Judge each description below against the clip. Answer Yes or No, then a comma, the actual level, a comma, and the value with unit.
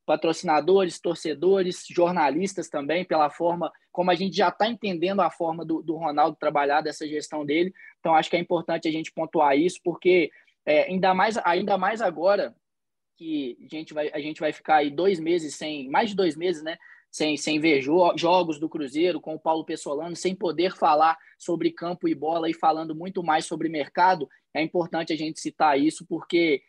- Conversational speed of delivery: No, fast, 190 wpm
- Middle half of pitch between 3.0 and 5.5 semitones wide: No, narrow, 2.6 semitones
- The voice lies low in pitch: No, medium, 165 Hz